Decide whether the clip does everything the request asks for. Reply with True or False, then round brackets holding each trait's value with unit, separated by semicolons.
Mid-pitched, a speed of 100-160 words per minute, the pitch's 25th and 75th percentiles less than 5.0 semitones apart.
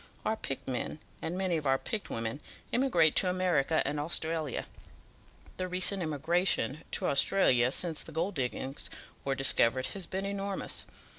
False (160 Hz; 150 wpm; 5.3 semitones)